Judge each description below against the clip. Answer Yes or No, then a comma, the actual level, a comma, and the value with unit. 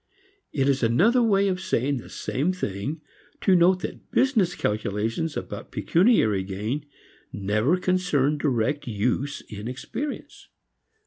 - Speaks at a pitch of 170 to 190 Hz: No, medium, 145 Hz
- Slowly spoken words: Yes, slow, 125 wpm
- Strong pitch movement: Yes, wide, 8.5 semitones